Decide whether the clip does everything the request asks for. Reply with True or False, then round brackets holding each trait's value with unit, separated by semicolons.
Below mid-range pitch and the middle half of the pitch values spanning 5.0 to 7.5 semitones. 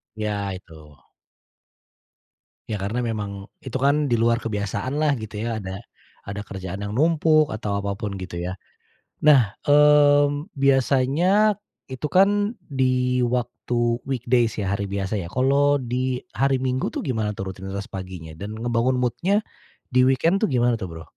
True (120 Hz; 5.6 semitones)